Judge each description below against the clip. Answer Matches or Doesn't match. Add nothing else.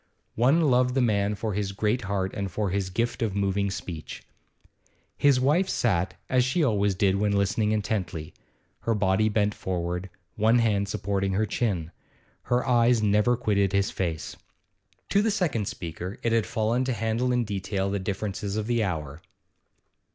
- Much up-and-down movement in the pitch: Doesn't match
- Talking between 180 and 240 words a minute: Doesn't match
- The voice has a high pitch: Doesn't match